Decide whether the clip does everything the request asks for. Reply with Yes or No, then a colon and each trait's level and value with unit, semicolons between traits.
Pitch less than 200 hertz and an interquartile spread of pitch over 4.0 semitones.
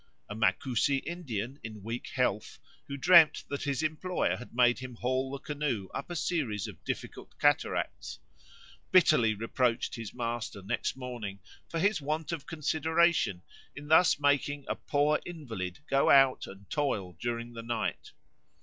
Yes: low, 135 Hz; average, 4.9 semitones